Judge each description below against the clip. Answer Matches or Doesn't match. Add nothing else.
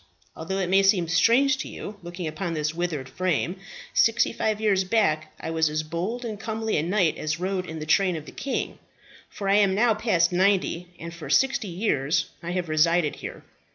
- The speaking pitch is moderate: Matches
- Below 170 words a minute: Doesn't match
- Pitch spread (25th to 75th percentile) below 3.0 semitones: Doesn't match